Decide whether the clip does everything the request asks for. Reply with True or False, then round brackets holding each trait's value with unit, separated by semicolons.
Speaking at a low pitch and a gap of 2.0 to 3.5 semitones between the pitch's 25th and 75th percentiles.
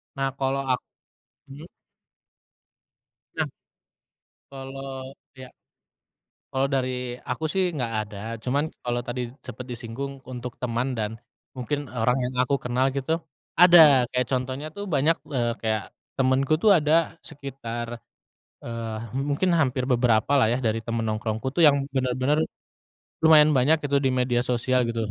True (130 Hz; 2.7 semitones)